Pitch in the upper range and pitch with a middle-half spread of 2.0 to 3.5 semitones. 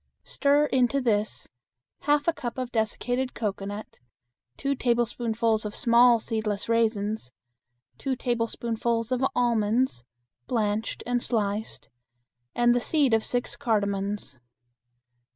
Yes: high, 230 Hz; narrow, 2.4 semitones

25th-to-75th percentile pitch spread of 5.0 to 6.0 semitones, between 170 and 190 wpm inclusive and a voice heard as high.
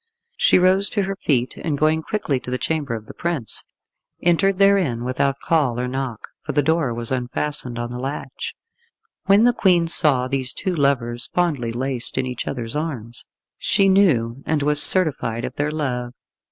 No: average, 5.3 semitones; average, 180 wpm; medium, 140 Hz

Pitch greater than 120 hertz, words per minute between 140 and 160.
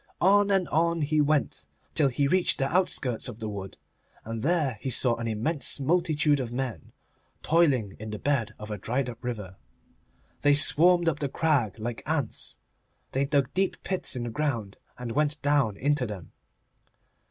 No: low, 135 Hz; average, 175 wpm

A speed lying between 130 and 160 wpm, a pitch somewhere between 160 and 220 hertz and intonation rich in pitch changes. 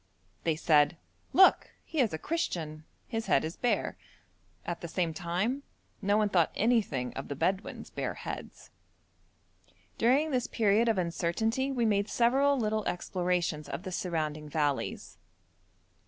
Yes: average, 140 wpm; high, 190 Hz; wide, 6.3 semitones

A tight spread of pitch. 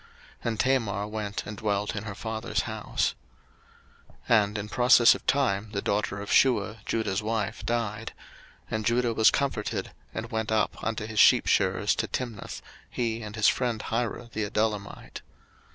Yes: narrow, 1.9 semitones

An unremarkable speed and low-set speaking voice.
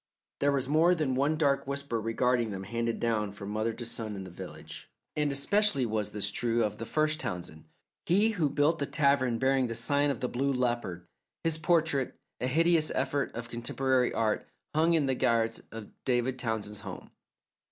Yes: average, 185 wpm; low, 125 Hz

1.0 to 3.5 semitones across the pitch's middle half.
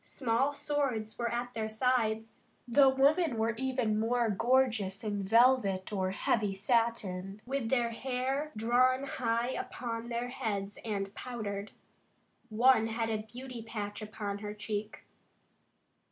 Yes: average, 3.1 semitones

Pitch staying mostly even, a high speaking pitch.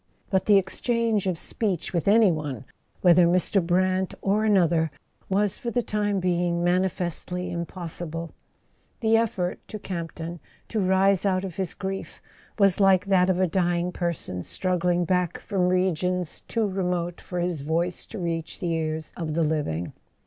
No: narrow, 2.2 semitones; medium, 180 Hz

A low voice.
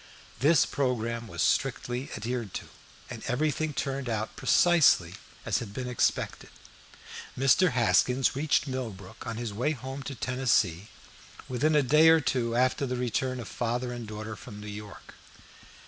Yes: low, 125 Hz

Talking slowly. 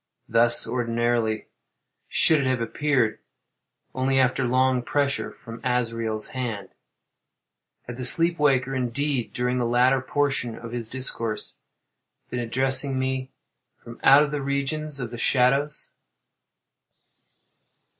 Yes: slow, 115 wpm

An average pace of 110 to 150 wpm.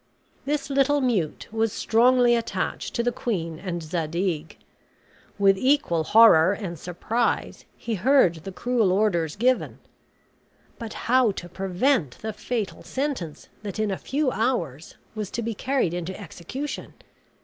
Yes: average, 140 wpm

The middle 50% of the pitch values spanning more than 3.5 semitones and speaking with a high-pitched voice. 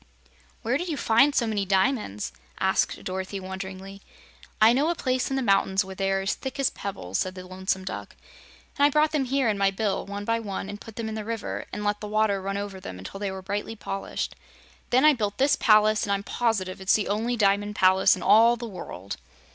No: average, 3.2 semitones; high, 205 Hz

